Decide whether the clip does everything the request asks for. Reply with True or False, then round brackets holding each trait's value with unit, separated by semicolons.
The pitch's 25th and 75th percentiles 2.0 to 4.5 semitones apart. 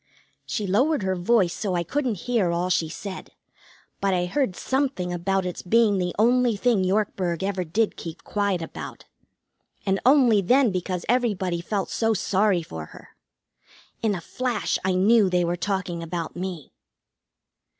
True (4.0 semitones)